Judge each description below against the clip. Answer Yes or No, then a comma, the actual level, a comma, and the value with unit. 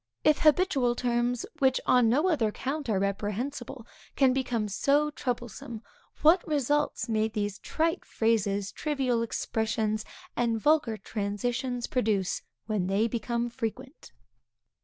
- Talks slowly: Yes, slow, 120 wpm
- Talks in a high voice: Yes, high, 240 Hz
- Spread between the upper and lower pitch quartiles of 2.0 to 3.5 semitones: No, average, 3.9 semitones